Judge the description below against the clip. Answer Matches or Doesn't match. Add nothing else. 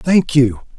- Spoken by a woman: Doesn't match